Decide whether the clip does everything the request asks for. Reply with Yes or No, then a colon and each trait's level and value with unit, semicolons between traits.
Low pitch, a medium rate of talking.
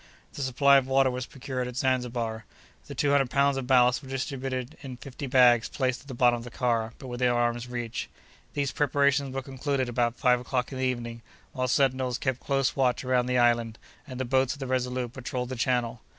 No: low, 125 Hz; fast, 210 wpm